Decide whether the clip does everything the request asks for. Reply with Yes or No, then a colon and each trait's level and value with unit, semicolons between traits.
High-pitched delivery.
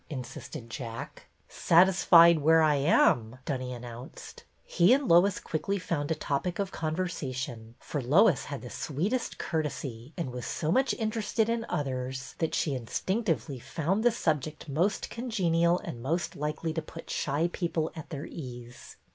No: medium, 155 Hz